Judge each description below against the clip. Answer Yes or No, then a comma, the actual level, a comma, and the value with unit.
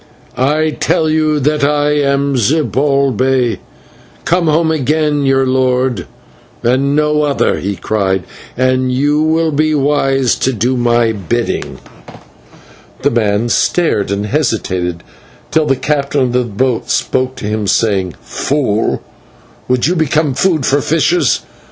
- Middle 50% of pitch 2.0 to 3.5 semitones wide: No, average, 4.0 semitones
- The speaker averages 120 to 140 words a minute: Yes, slow, 135 wpm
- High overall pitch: No, low, 135 Hz